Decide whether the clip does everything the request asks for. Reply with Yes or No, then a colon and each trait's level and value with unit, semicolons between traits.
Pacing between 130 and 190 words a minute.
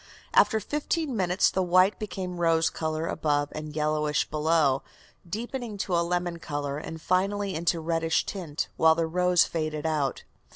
Yes: average, 150 wpm